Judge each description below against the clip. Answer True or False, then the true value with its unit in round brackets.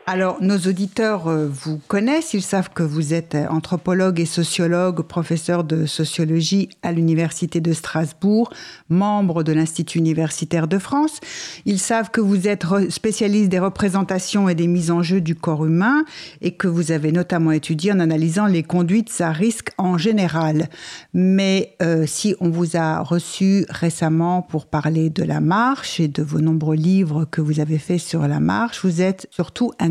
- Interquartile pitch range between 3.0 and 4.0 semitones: True (3.3 semitones)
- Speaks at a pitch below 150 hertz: False (175 Hz)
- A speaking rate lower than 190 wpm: True (170 wpm)